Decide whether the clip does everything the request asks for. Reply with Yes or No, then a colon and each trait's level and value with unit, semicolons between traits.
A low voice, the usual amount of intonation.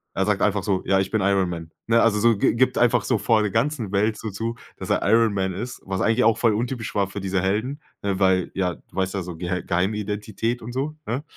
Yes: low, 105 Hz; average, 3.2 semitones